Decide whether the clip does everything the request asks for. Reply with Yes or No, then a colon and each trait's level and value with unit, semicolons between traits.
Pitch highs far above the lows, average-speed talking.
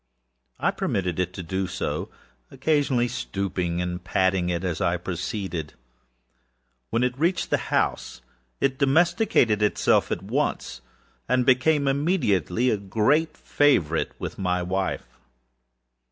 No: wide, 6.9 semitones; slow, 125 wpm